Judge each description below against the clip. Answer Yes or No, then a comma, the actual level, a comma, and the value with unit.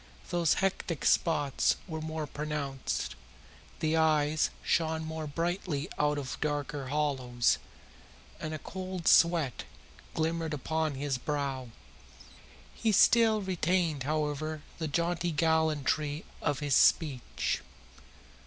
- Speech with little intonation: Yes, narrow, 2.2 semitones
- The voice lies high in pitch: No, medium, 155 Hz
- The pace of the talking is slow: Yes, slow, 105 wpm